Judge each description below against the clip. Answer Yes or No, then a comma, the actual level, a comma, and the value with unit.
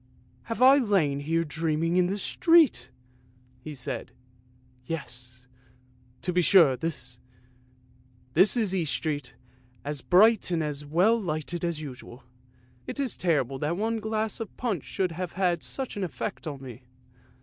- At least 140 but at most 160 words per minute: Yes, average, 150 wpm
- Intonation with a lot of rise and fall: Yes, wide, 6.0 semitones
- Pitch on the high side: No, medium, 165 Hz